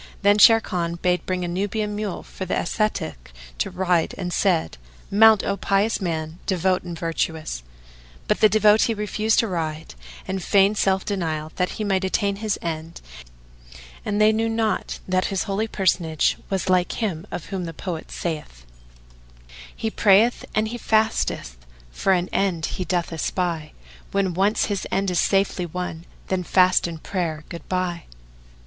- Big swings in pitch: No, average, 3.3 semitones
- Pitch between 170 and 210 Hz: Yes, medium, 185 Hz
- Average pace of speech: Yes, average, 165 wpm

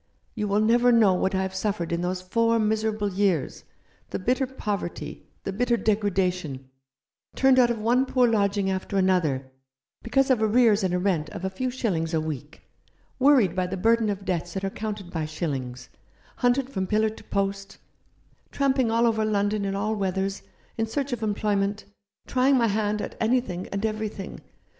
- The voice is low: No, high, 205 Hz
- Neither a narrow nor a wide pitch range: Yes, average, 3.5 semitones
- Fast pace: No, average, 175 wpm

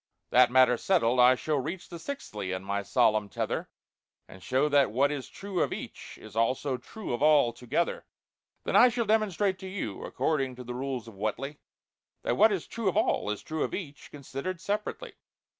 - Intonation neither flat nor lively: No, wide, 7.3 semitones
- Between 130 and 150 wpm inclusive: No, average, 190 wpm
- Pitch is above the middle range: No, medium, 140 Hz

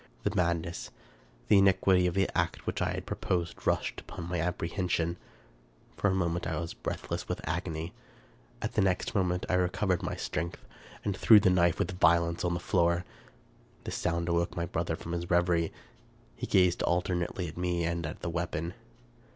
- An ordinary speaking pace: Yes, average, 180 wpm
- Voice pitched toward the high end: No, very low, 85 Hz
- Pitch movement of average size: No, narrow, 1.3 semitones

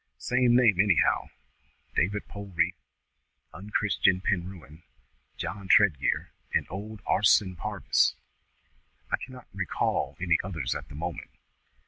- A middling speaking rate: No, slow, 105 wpm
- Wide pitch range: No, average, 3.1 semitones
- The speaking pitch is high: No, very low, 95 Hz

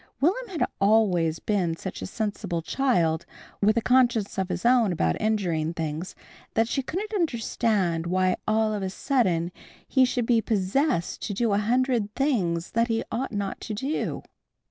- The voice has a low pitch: No, high, 215 Hz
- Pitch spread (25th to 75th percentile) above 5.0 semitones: Yes, wide, 5.4 semitones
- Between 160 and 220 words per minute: Yes, average, 165 wpm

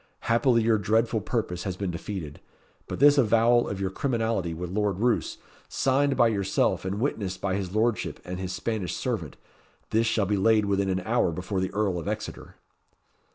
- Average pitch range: Yes, average, 3.5 semitones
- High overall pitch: No, low, 105 Hz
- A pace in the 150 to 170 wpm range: No, average, 180 wpm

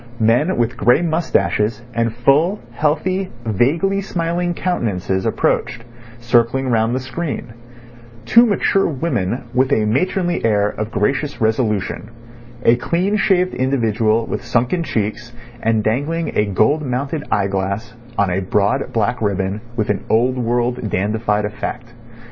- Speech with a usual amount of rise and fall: No, wide, 6.0 semitones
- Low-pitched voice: Yes, low, 120 Hz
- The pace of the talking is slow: Yes, slow, 130 wpm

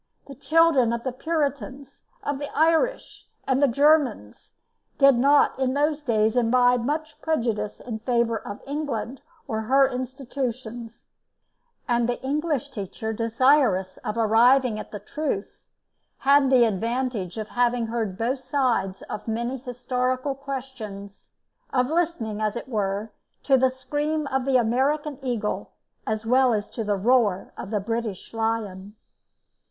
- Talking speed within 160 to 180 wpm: No, average, 140 wpm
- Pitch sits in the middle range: No, high, 245 Hz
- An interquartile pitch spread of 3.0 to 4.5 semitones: Yes, average, 3.7 semitones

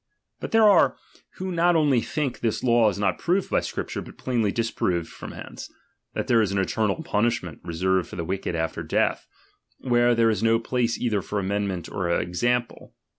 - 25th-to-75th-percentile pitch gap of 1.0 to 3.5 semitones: No, average, 4.4 semitones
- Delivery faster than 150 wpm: Yes, average, 185 wpm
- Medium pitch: No, low, 115 Hz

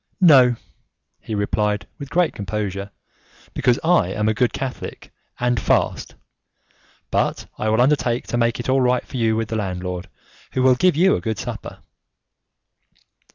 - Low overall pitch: Yes, low, 115 Hz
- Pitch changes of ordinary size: Yes, average, 3.5 semitones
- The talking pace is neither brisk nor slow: Yes, average, 155 wpm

